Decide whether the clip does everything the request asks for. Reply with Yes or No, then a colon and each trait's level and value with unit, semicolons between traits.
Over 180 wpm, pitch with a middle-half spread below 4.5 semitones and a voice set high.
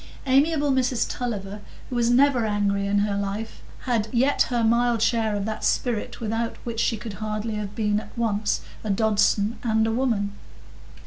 No: average, 175 wpm; narrow, 2.5 semitones; high, 220 Hz